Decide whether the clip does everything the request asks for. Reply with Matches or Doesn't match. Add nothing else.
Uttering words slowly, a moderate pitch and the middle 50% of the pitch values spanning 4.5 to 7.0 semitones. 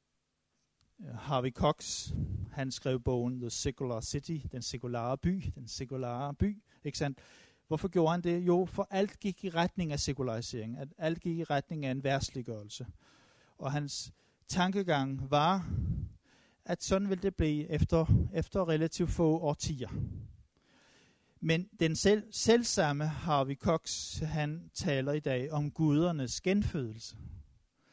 Matches